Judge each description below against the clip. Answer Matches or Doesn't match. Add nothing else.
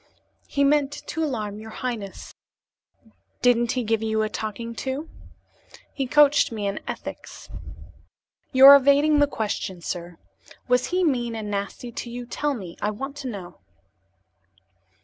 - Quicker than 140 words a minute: Matches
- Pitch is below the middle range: Doesn't match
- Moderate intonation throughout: Matches